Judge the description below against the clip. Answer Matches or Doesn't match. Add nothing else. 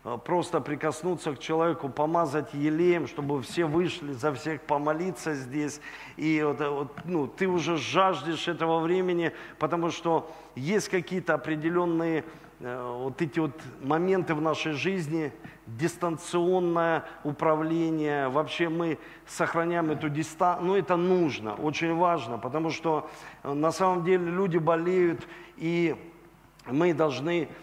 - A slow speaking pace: Doesn't match